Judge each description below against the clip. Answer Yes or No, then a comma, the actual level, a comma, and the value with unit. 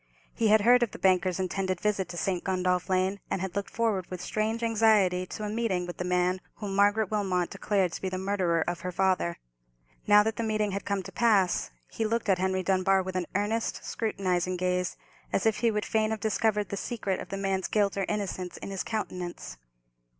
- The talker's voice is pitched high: Yes, high, 195 Hz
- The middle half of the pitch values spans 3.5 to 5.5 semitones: No, narrow, 2.6 semitones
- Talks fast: Yes, fast, 215 wpm